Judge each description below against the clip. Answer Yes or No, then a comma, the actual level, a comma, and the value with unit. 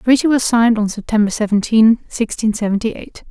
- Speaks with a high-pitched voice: Yes, high, 220 Hz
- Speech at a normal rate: Yes, average, 180 wpm